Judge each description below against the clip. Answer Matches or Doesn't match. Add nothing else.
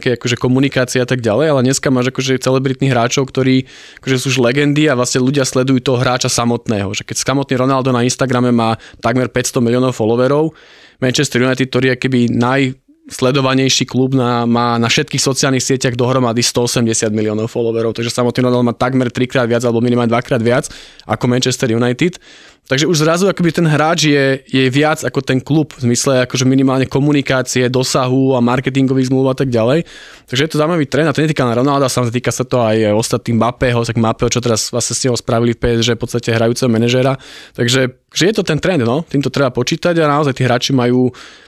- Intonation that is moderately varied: Doesn't match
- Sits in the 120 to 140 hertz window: Matches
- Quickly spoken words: Matches